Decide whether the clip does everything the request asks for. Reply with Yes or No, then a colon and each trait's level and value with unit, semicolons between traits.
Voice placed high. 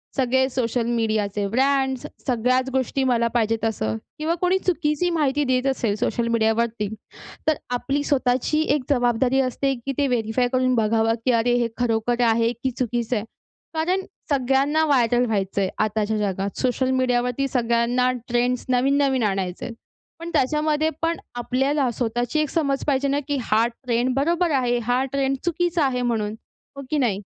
Yes: very high, 250 Hz